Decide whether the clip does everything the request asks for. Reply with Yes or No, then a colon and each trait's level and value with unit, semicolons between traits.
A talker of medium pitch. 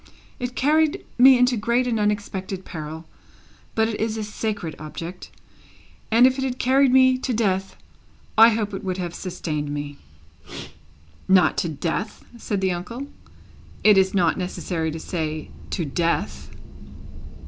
No: high, 195 Hz